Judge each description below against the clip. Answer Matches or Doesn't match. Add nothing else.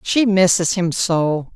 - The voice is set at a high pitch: Doesn't match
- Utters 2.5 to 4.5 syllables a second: Matches